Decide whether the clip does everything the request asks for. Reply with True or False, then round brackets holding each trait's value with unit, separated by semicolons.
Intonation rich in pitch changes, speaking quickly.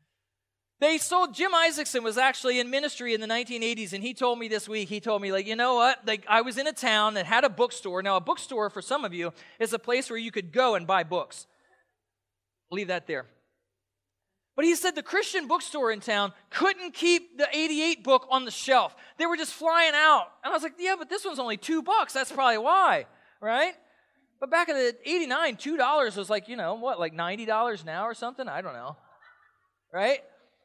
True (6.8 semitones; 220 wpm)